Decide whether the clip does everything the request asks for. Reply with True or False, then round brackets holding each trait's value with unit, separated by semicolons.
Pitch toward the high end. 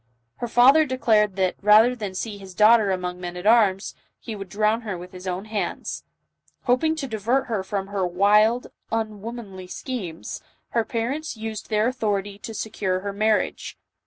True (210 Hz)